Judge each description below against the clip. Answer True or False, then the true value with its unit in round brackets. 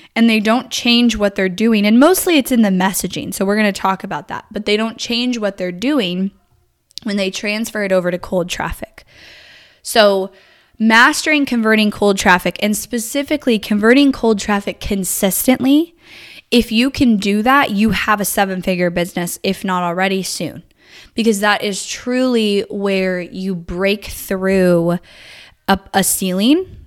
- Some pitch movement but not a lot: True (3.6 semitones)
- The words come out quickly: False (160 wpm)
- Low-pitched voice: False (205 Hz)